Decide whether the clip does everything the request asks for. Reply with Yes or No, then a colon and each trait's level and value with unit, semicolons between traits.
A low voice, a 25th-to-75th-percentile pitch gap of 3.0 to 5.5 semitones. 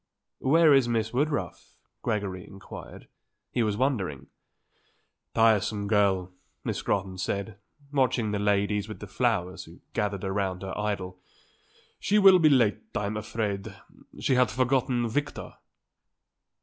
Yes: low, 105 Hz; average, 4.1 semitones